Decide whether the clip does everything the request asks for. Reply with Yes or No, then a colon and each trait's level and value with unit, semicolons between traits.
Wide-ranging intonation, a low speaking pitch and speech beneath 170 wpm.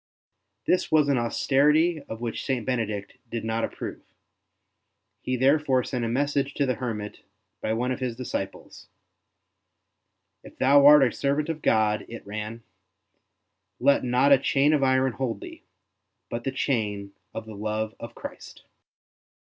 No: average, 3.8 semitones; low, 125 Hz; average, 155 wpm